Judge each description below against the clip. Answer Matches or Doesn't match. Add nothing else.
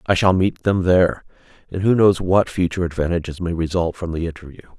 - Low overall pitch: Matches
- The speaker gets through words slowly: Doesn't match